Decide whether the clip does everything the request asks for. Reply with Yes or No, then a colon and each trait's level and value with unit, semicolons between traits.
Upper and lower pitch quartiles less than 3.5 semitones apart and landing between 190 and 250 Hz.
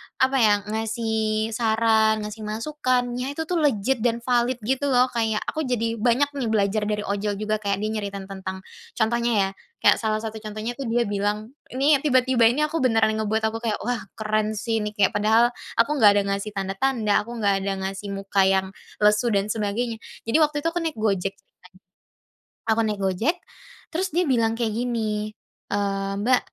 Yes: average, 2.9 semitones; high, 220 Hz